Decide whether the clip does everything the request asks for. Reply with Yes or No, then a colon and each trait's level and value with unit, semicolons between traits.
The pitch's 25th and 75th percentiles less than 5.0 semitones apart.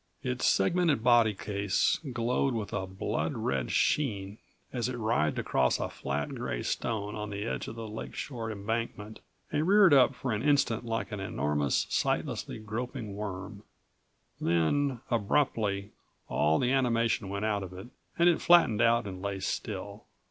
Yes: average, 3.7 semitones